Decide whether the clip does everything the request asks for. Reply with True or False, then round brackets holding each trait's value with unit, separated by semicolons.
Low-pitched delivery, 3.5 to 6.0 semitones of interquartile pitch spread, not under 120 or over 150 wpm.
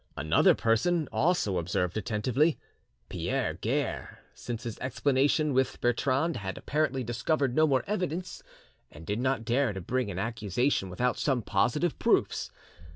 True (125 Hz; 5.1 semitones; 140 wpm)